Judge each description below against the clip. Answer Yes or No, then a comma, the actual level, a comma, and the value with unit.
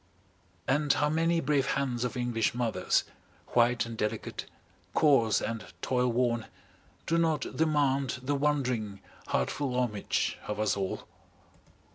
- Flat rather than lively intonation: No, average, 4.0 semitones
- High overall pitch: No, low, 125 Hz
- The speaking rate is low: Yes, slow, 130 wpm